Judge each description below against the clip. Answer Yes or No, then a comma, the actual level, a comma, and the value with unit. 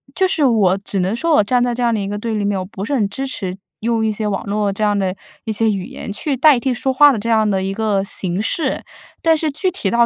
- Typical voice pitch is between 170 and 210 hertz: No, high, 220 Hz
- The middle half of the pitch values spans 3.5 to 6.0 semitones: Yes, average, 4.0 semitones